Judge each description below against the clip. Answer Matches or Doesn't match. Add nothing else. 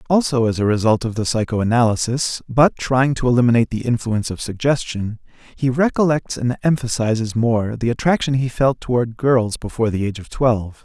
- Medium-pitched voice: Doesn't match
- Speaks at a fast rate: Doesn't match